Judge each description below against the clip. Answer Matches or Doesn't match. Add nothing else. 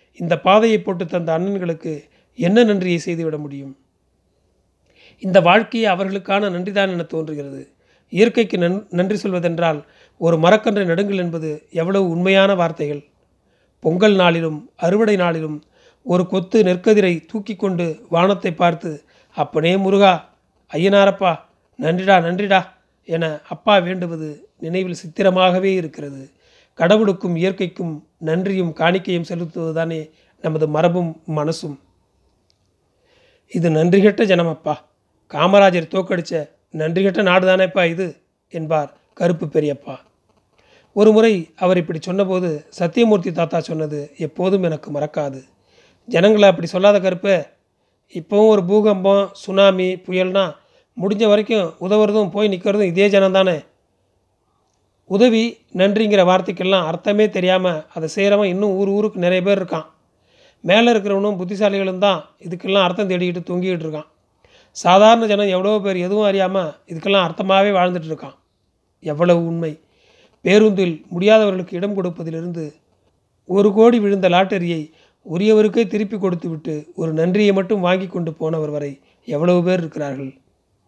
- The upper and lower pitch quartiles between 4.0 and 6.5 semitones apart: Doesn't match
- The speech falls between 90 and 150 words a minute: Matches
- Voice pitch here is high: Doesn't match